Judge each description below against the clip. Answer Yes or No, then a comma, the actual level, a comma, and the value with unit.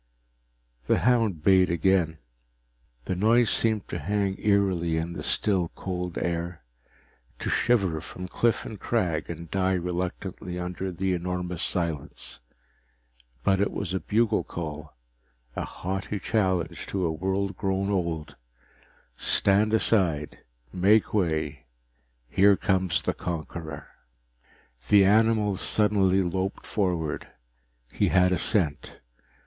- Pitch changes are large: No, average, 2.8 semitones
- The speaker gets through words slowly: Yes, slow, 120 wpm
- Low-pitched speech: Yes, very low, 95 Hz